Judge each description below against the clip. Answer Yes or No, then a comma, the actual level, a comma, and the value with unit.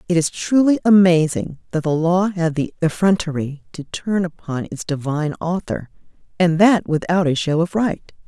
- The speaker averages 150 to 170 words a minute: Yes, average, 165 wpm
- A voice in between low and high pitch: Yes, medium, 170 Hz